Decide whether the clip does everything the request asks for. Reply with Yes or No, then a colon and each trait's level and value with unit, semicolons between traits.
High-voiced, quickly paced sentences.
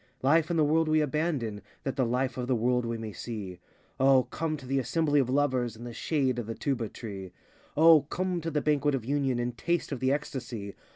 No: low, 130 Hz; fast, 225 wpm